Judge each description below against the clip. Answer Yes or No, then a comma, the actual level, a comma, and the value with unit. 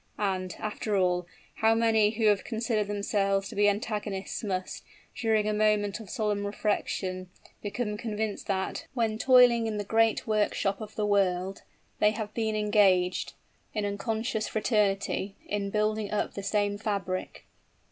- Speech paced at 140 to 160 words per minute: Yes, average, 145 wpm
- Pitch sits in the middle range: No, high, 210 Hz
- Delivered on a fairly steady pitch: Yes, narrow, 1.6 semitones